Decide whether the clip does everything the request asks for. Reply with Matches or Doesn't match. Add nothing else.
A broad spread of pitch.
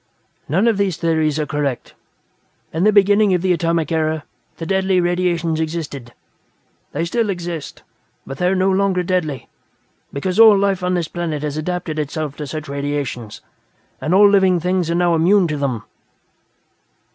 Doesn't match